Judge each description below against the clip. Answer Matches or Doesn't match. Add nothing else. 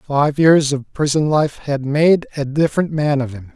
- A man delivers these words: Matches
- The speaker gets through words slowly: Doesn't match